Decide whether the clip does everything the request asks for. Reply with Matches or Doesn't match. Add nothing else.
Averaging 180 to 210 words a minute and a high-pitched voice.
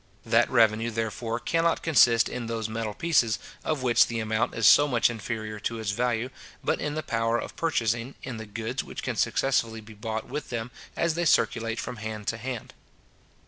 Doesn't match